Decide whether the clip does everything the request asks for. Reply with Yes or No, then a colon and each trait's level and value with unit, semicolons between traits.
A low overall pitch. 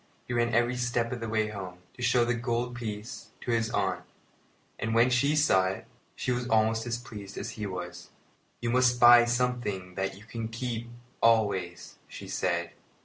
Yes: low, 115 Hz